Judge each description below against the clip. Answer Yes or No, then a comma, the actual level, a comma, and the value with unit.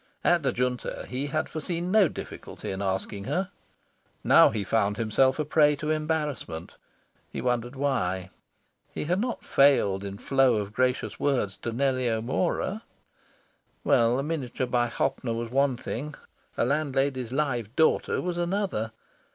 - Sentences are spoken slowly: No, average, 150 wpm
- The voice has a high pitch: No, low, 130 Hz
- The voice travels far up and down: No, average, 4.8 semitones